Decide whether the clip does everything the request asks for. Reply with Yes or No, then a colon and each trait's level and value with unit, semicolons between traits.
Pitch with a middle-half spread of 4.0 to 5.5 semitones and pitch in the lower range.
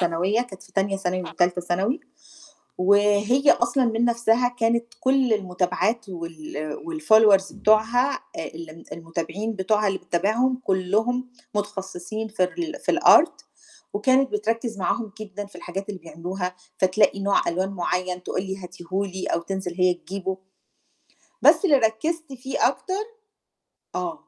No: average, 4.3 semitones; high, 200 Hz